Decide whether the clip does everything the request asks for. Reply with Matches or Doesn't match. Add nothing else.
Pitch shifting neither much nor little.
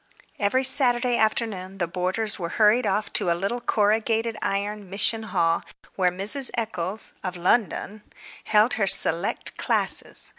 Matches